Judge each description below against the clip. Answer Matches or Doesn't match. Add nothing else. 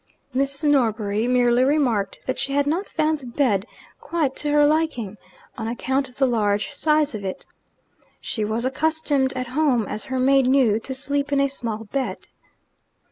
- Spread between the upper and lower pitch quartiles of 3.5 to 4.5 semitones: Matches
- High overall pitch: Matches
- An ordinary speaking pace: Matches